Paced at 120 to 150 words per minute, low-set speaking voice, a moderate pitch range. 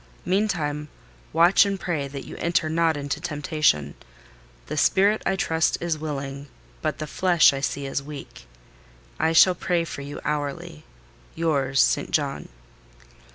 No: average, 140 wpm; medium, 155 Hz; average, 3.4 semitones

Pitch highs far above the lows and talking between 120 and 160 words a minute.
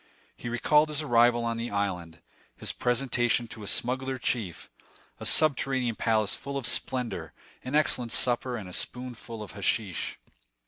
No: average, 2.9 semitones; average, 150 wpm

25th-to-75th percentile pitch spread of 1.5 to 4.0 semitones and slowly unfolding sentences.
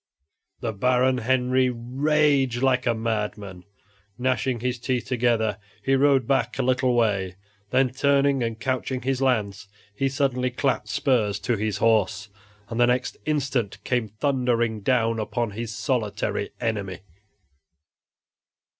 Yes: average, 2.8 semitones; slow, 130 wpm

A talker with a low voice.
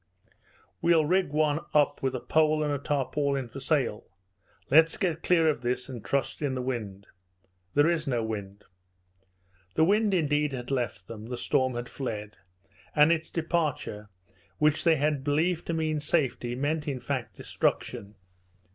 No: medium, 145 Hz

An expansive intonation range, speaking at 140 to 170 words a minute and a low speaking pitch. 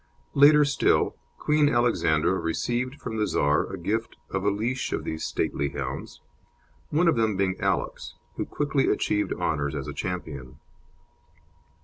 Yes: wide, 8.8 semitones; average, 145 wpm; low, 105 Hz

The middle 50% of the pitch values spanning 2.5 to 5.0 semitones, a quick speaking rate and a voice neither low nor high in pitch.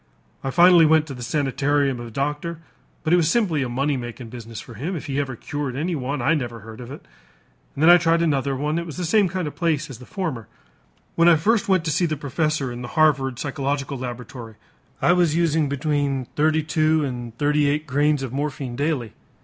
Yes: average, 3.5 semitones; fast, 220 wpm; medium, 145 Hz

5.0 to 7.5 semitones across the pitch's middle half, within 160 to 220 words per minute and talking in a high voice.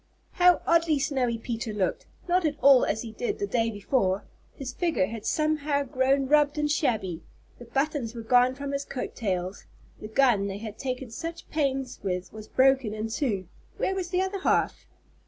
Yes: wide, 5.4 semitones; average, 185 wpm; very high, 260 Hz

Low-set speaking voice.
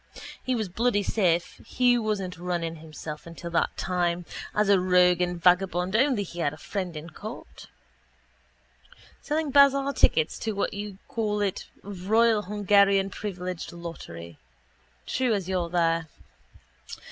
No: medium, 185 Hz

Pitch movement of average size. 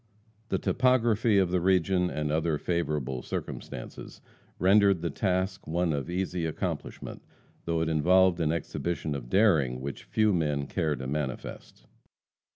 Yes: average, 3.9 semitones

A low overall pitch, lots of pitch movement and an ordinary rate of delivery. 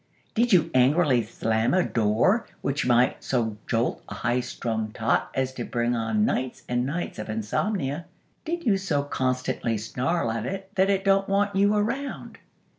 Yes: low, 130 Hz; wide, 8.8 semitones; average, 170 wpm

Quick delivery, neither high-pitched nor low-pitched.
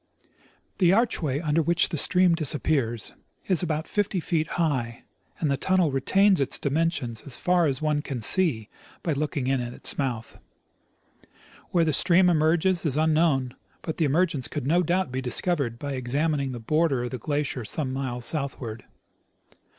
No: average, 165 wpm; medium, 150 Hz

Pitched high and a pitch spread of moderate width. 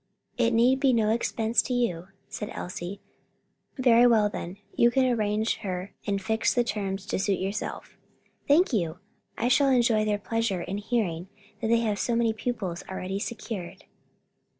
Yes: high, 220 Hz; average, 3.4 semitones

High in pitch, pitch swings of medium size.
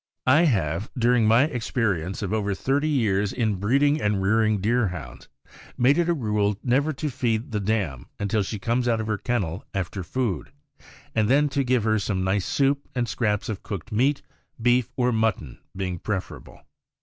No: low, 110 Hz; average, 4.1 semitones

